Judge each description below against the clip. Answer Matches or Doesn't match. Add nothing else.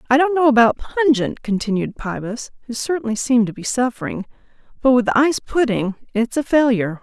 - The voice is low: Doesn't match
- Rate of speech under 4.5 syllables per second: Doesn't match